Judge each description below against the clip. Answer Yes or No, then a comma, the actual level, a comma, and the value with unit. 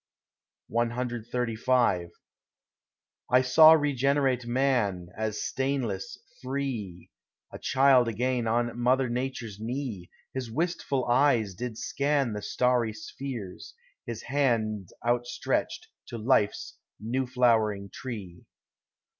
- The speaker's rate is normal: No, slow, 95 wpm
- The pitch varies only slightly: No, average, 3.2 semitones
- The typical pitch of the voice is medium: No, low, 120 Hz